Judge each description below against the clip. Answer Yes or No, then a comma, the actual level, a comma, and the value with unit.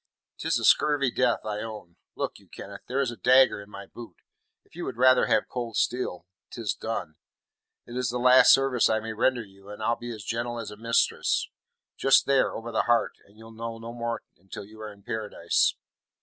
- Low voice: Yes, low, 115 Hz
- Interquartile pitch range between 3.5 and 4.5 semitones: No, average, 2.7 semitones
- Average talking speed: No, fast, 210 wpm